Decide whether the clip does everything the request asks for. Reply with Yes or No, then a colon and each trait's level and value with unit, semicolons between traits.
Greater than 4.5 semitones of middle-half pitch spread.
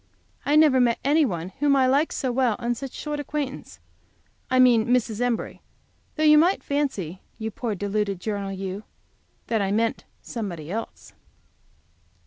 Yes: average, 5.3 semitones